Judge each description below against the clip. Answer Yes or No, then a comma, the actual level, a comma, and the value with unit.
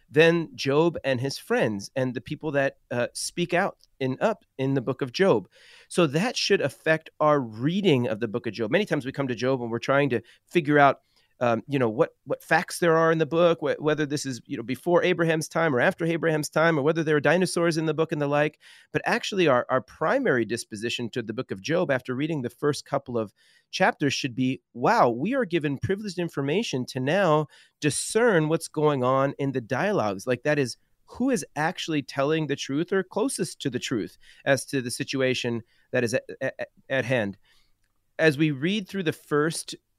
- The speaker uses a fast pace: Yes, fast, 215 wpm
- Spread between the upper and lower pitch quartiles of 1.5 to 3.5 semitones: No, average, 4.2 semitones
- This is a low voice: No, medium, 145 Hz